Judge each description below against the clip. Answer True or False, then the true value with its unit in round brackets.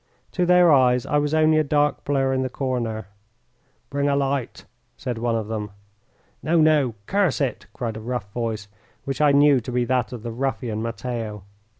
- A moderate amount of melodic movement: True (3.9 semitones)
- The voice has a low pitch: True (130 Hz)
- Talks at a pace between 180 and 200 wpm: True (190 wpm)